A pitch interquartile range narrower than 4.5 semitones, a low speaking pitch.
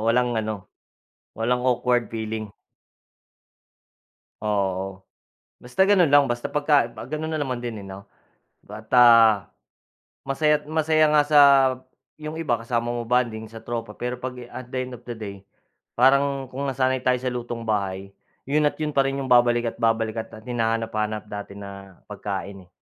Yes: average, 3.7 semitones; low, 120 Hz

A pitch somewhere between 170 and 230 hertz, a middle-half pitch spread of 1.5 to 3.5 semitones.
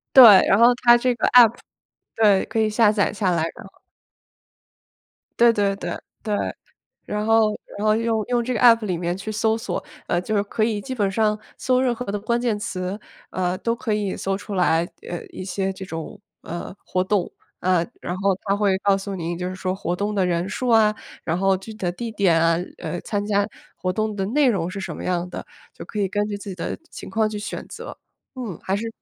Yes: high, 205 Hz; average, 3.1 semitones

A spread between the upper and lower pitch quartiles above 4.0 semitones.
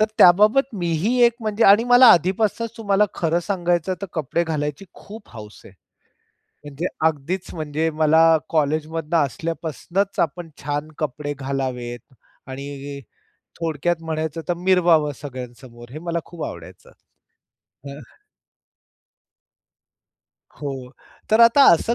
Yes: average, 4.7 semitones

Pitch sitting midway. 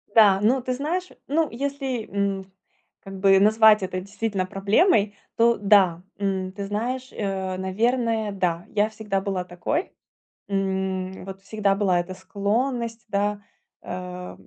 No: high, 200 Hz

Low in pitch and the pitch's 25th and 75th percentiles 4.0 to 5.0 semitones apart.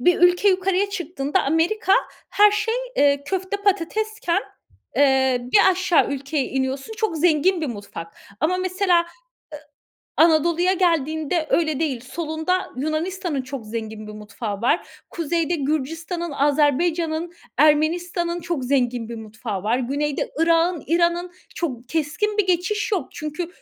No: very high, 320 Hz; average, 4.5 semitones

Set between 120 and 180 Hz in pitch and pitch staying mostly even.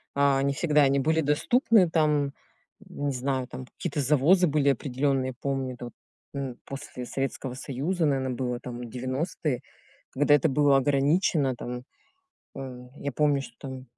Yes: medium, 140 Hz; narrow, 2.3 semitones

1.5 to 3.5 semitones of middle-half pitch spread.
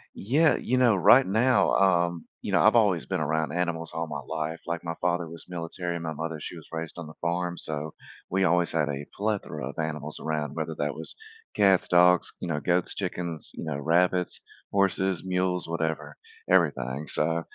Yes: narrow, 2.4 semitones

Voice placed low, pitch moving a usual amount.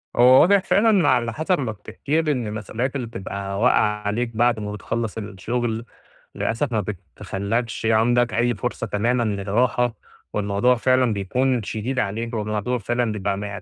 Yes: low, 115 Hz; average, 3.1 semitones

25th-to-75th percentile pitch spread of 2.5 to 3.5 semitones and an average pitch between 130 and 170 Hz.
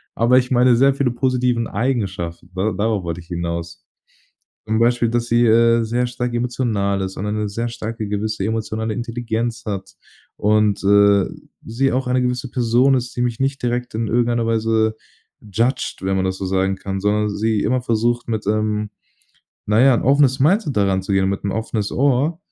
No: average, 3.2 semitones; low, 115 Hz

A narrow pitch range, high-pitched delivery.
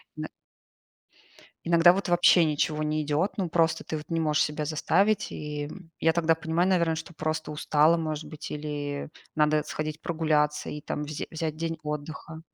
No: narrow, 1.7 semitones; medium, 155 Hz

